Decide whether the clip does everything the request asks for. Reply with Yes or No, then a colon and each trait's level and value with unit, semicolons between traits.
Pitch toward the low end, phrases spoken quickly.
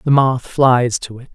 Yes: low, 125 Hz; fast, 220 wpm